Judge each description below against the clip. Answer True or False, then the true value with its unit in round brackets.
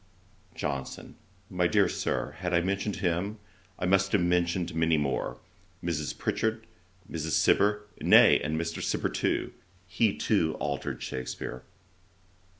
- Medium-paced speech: False (130 wpm)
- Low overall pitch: True (85 Hz)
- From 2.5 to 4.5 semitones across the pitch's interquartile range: True (3.9 semitones)